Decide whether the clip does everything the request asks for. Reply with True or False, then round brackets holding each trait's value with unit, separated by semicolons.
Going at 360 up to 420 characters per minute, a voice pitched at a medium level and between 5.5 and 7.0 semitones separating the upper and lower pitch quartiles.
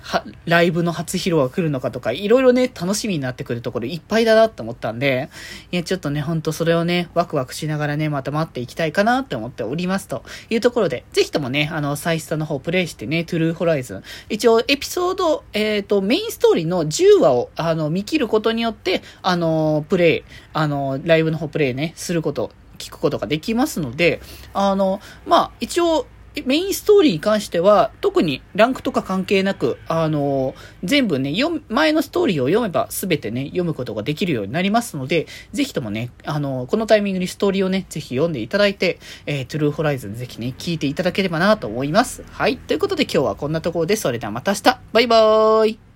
False (455 characters per minute; 175 Hz; 6.4 semitones)